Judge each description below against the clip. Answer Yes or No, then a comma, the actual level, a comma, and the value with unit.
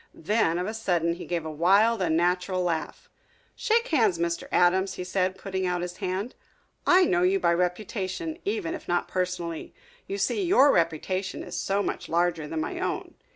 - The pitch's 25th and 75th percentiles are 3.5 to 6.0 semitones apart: Yes, average, 4.4 semitones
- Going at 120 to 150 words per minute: No, average, 180 wpm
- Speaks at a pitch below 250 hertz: Yes, medium, 185 Hz